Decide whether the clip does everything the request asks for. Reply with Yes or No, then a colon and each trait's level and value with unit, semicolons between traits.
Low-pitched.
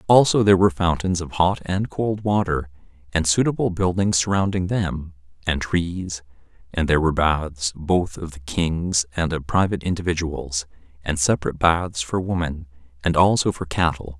Yes: very low, 85 Hz